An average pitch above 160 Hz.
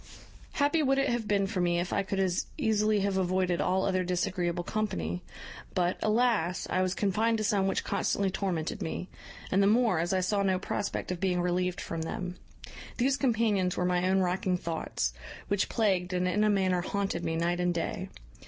Yes: medium, 185 Hz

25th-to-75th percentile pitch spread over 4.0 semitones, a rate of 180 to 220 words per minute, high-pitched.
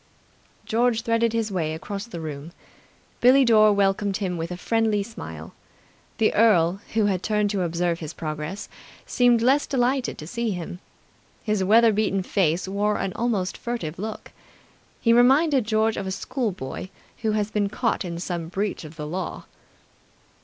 No: average, 4.4 semitones; average, 160 wpm; high, 205 Hz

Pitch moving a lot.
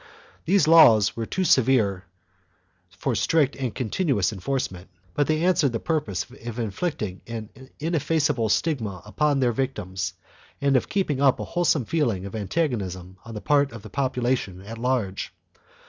Yes: wide, 6.2 semitones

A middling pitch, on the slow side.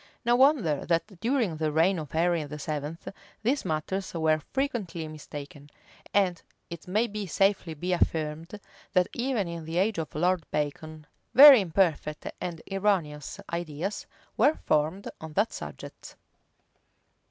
Yes: medium, 170 Hz; slow, 130 wpm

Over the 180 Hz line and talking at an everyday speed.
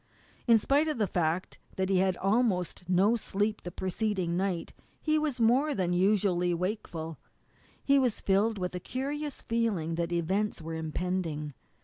Yes: high, 190 Hz; average, 160 wpm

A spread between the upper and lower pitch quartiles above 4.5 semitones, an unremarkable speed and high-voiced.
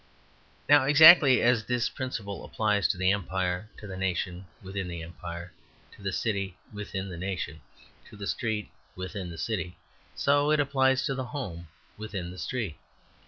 No: wide, 5.6 semitones; average, 165 wpm; low, 100 Hz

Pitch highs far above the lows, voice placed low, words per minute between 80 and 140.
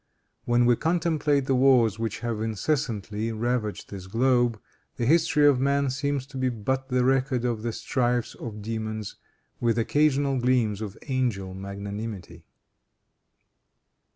No: average, 3.6 semitones; low, 120 Hz; slow, 135 wpm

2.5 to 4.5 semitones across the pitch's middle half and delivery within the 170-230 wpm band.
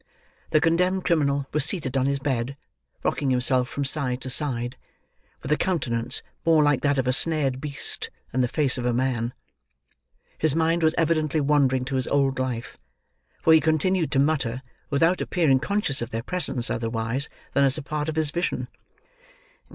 Yes: average, 3.5 semitones; average, 175 wpm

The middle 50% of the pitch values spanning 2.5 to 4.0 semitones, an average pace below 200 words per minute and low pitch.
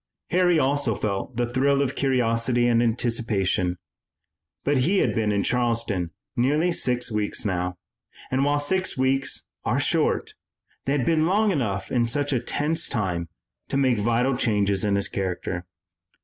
No: average, 5.1 semitones; average, 155 wpm; low, 120 Hz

